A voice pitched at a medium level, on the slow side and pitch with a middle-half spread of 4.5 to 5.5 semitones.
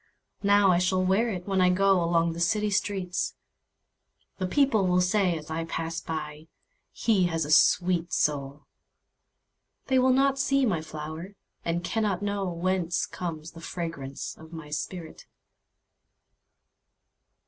No: medium, 180 Hz; slow, 115 wpm; average, 3.4 semitones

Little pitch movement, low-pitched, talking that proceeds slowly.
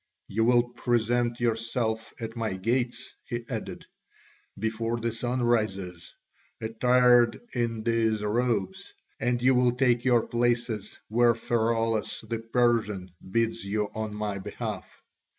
Yes: narrow, 1.8 semitones; low, 115 Hz; slow, 125 wpm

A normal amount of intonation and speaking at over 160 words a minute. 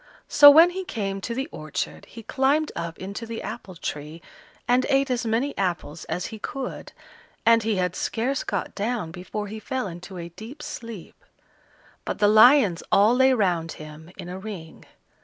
No: wide, 5.7 semitones; average, 175 wpm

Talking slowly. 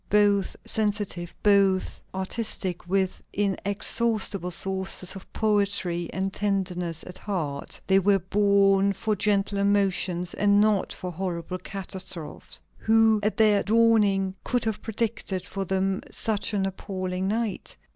Yes: slow, 125 wpm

